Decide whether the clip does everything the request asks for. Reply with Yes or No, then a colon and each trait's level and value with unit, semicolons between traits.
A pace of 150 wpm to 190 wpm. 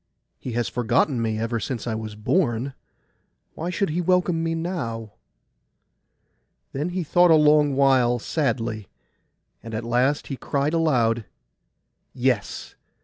No: average, 140 wpm